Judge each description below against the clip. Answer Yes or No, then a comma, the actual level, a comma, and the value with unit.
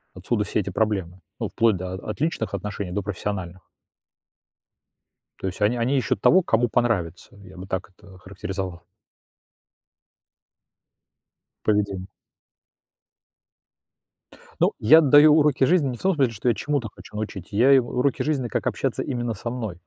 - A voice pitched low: Yes, low, 110 Hz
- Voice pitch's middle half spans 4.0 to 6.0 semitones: Yes, average, 5.1 semitones